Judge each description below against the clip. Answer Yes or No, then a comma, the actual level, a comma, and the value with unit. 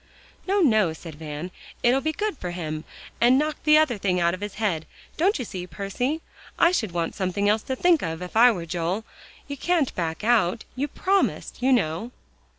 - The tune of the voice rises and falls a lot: Yes, wide, 7.9 semitones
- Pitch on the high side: Yes, high, 215 Hz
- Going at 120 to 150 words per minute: No, average, 200 wpm